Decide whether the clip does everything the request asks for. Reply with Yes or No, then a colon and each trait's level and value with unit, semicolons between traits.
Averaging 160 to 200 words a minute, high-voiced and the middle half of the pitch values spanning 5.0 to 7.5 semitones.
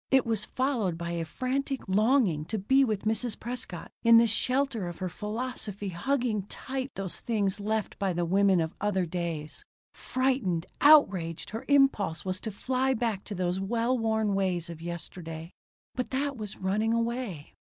Yes: average, 165 wpm; high, 210 Hz; wide, 5.5 semitones